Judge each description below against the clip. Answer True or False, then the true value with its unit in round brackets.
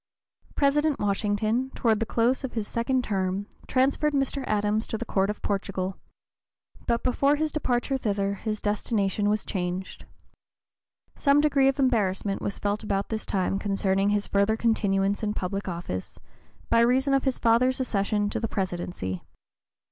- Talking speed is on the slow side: False (155 wpm)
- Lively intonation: False (4.4 semitones)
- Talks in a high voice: True (215 Hz)